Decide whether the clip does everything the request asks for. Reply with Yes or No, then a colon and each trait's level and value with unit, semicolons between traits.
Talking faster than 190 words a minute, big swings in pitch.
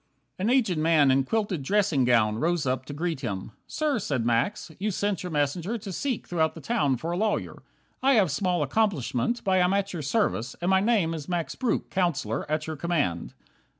Yes: fast, 205 wpm; wide, 6.3 semitones